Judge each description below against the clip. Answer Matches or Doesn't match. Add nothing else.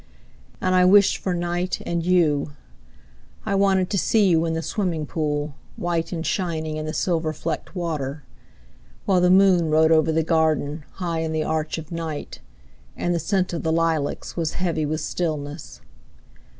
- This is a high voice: Doesn't match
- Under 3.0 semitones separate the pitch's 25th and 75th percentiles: Matches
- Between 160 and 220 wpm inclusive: Matches